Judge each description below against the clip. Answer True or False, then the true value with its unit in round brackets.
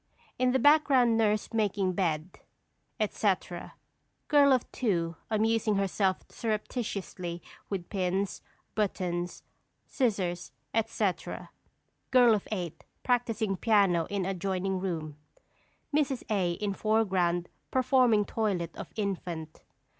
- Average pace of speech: False (100 wpm)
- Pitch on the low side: False (200 Hz)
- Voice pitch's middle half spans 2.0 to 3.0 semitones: False (3.9 semitones)